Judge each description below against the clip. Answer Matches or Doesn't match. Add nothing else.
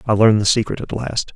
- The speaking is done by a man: Matches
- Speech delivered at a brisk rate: Matches